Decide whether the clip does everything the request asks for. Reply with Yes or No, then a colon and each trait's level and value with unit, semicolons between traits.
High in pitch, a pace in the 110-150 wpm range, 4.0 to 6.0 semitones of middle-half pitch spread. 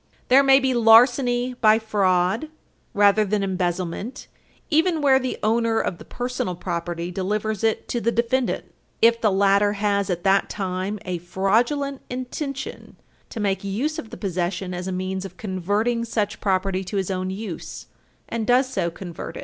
No: high, 205 Hz; average, 165 wpm; average, 4.4 semitones